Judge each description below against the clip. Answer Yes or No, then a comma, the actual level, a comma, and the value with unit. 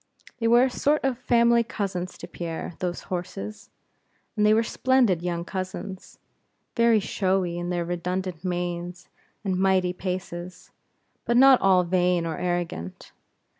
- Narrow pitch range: No, average, 3.6 semitones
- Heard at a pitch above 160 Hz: Yes, medium, 185 Hz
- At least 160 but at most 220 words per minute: No, average, 145 wpm